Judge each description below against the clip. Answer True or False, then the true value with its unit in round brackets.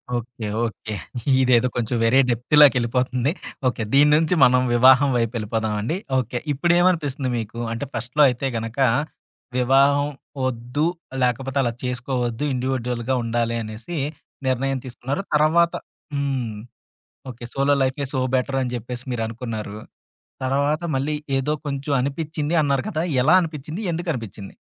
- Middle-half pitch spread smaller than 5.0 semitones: True (3.2 semitones)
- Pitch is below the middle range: True (130 Hz)